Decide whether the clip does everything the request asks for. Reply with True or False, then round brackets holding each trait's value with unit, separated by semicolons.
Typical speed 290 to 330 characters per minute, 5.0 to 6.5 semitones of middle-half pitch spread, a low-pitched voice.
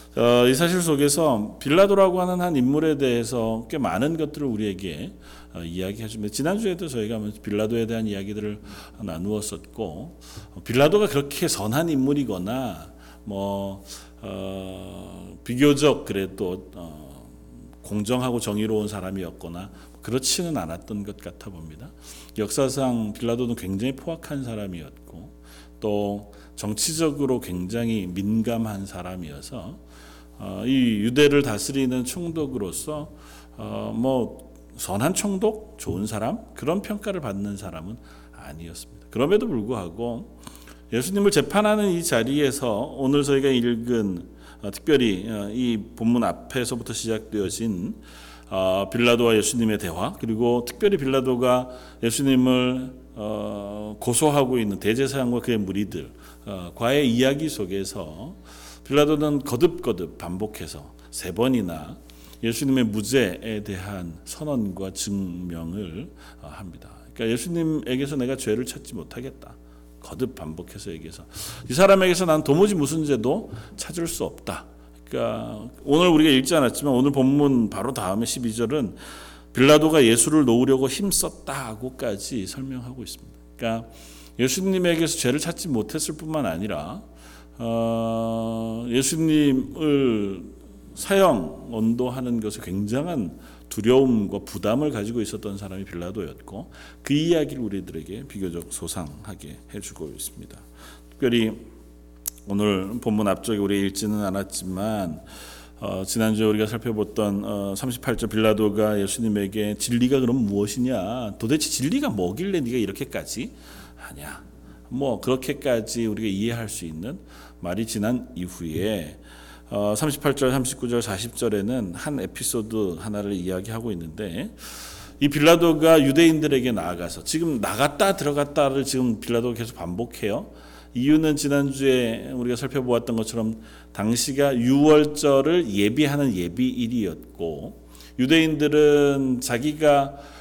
True (295 characters per minute; 6.1 semitones; 115 Hz)